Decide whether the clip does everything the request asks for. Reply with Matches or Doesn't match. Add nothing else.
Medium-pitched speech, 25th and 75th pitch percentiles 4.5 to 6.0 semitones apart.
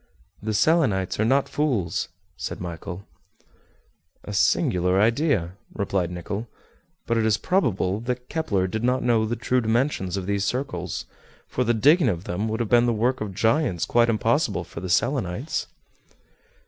Doesn't match